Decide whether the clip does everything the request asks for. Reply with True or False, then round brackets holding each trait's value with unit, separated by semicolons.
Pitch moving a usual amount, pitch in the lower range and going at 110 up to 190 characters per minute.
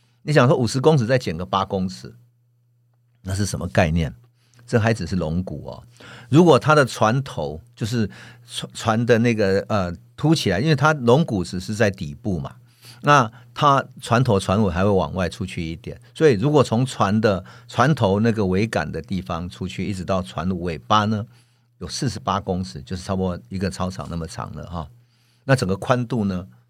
False (4.3 semitones; 115 Hz; 270 characters per minute)